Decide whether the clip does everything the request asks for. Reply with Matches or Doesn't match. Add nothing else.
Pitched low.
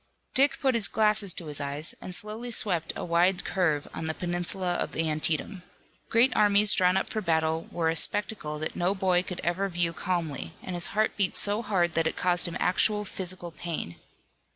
Doesn't match